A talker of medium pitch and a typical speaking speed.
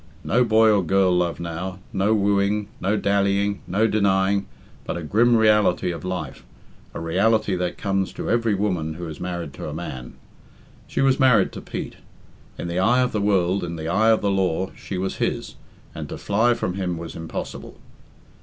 No: very low, 95 Hz; average, 190 wpm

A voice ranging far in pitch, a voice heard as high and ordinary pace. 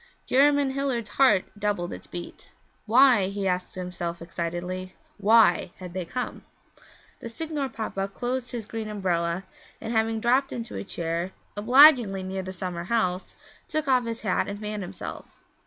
No: average, 4.8 semitones; high, 210 Hz; average, 155 wpm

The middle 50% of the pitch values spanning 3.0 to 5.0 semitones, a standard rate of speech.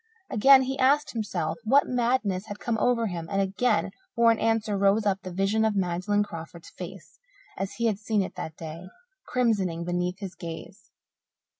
Yes: average, 4.0 semitones; average, 175 wpm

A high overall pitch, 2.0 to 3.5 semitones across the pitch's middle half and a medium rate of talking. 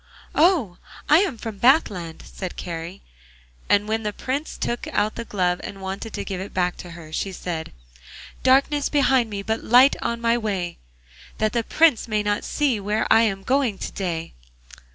No: high, 215 Hz; average, 4.5 semitones; average, 175 wpm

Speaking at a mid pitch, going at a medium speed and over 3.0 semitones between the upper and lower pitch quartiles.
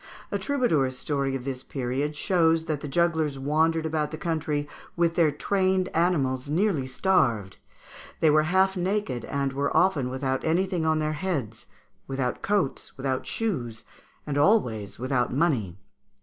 Yes: medium, 150 Hz; average, 150 wpm; average, 4.5 semitones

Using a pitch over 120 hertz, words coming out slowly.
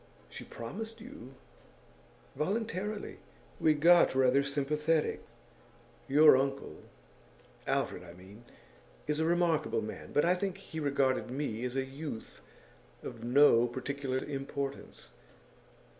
Yes: medium, 140 Hz; slow, 115 wpm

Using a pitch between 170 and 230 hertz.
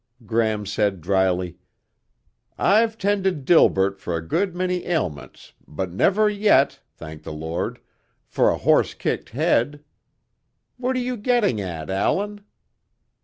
No: low, 120 Hz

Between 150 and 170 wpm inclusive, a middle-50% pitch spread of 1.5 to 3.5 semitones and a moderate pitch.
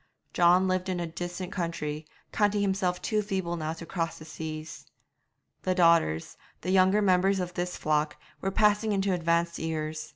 Yes: average, 165 wpm; average, 2.8 semitones; medium, 175 Hz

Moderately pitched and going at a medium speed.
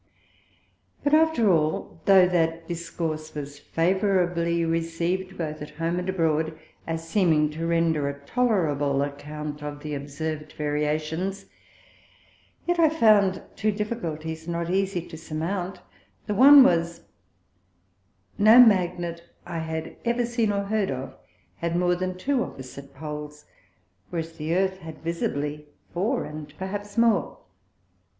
No: medium, 170 Hz; slow, 130 wpm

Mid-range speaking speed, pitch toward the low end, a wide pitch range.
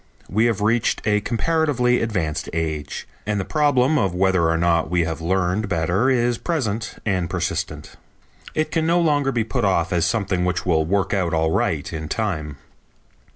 Yes: average, 175 wpm; low, 100 Hz; wide, 6.0 semitones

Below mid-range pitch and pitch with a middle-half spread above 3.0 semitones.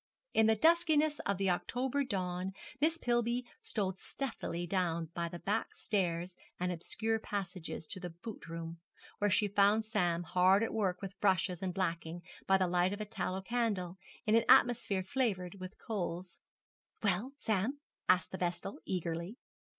No: high, 190 Hz; average, 3.8 semitones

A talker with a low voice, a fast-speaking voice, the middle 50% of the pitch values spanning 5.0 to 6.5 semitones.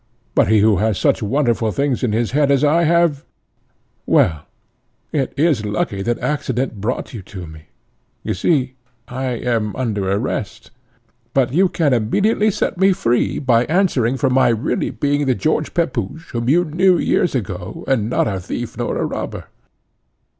No: low, 125 Hz; average, 170 wpm; wide, 5.5 semitones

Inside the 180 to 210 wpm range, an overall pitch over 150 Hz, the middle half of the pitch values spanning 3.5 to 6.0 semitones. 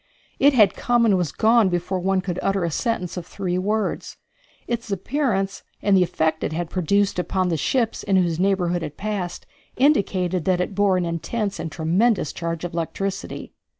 No: average, 185 wpm; medium, 185 Hz; average, 2.7 semitones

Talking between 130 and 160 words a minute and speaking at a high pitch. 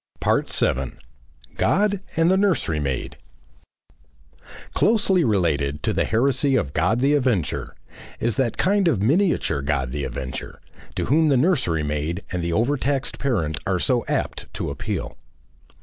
No: average, 140 wpm; low, 115 Hz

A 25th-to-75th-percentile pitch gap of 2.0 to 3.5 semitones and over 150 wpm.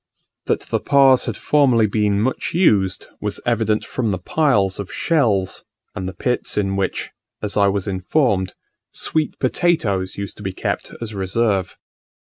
No: average, 4.6 semitones; average, 160 wpm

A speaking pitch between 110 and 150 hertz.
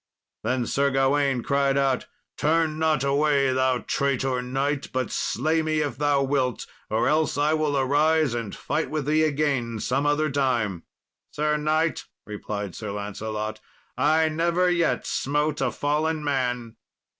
Yes: medium, 140 Hz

